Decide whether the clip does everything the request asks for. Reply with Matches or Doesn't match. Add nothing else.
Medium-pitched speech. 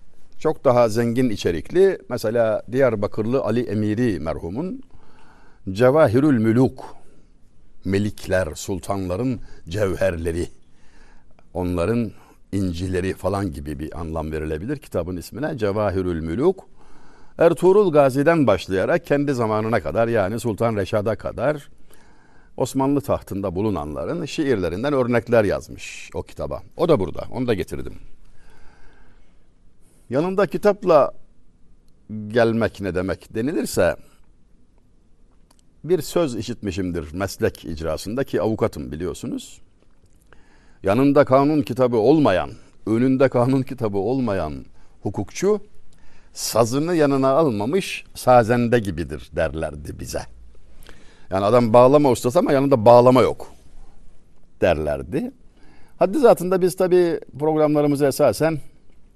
Doesn't match